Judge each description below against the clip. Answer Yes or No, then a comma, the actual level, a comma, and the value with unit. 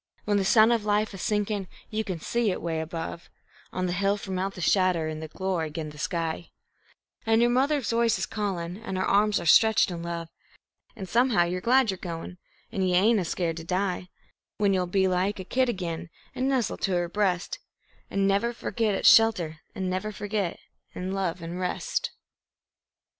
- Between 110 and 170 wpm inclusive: No, average, 195 wpm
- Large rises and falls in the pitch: No, average, 3.5 semitones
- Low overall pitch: No, high, 190 Hz